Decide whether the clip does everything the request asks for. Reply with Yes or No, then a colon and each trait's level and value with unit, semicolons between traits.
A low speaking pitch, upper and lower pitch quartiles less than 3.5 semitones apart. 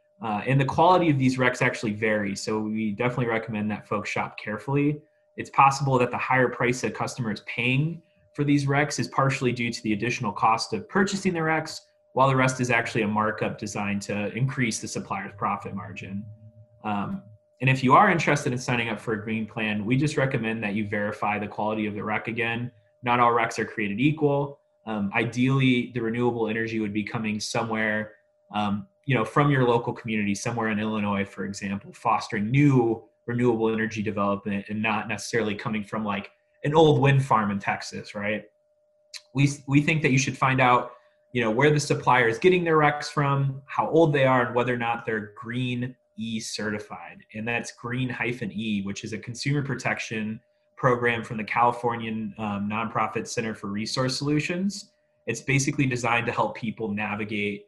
No: low, 120 Hz; average, 4.1 semitones